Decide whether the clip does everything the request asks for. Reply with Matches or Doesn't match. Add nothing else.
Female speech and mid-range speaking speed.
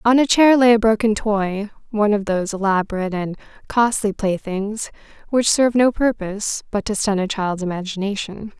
Matches